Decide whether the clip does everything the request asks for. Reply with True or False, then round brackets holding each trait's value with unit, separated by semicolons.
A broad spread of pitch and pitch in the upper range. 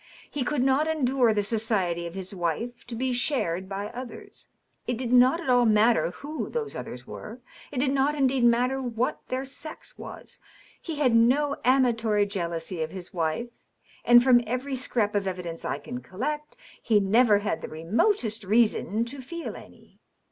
False (4.5 semitones; 240 Hz)